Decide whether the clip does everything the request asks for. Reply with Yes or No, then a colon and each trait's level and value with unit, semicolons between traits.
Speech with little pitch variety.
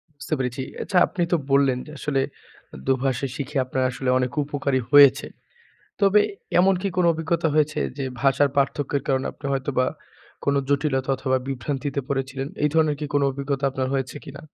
Yes: narrow, 1.8 semitones